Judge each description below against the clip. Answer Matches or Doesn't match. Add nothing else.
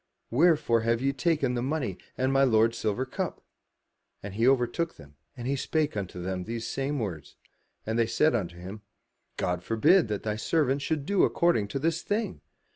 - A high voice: Doesn't match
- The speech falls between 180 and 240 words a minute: Matches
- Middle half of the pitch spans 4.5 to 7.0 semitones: Matches